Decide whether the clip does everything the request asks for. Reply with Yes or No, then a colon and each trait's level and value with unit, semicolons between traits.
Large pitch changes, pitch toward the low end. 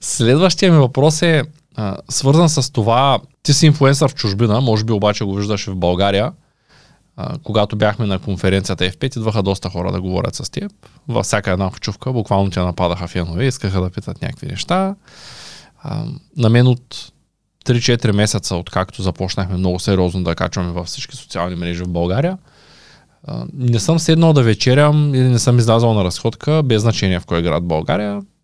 Yes: wide, 6.3 semitones; low, 110 Hz